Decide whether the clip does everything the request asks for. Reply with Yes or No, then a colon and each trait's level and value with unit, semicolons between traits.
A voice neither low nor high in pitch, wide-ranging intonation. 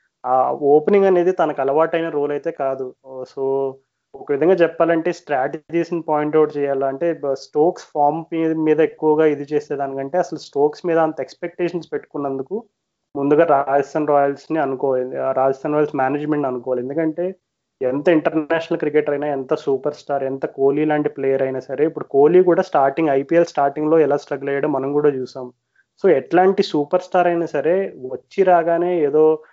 No: medium, 150 Hz; average, 3.6 semitones